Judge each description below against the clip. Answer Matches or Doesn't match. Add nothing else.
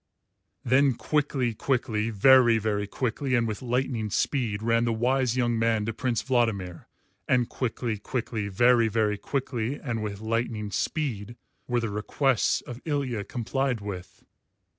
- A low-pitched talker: Matches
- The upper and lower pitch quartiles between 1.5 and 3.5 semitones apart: Matches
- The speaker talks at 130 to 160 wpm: Matches